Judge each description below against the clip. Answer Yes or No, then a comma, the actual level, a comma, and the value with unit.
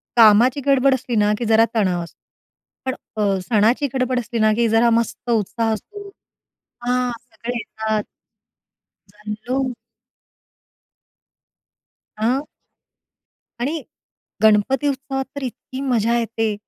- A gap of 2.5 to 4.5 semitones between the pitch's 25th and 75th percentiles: Yes, average, 3.1 semitones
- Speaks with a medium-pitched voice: No, high, 235 Hz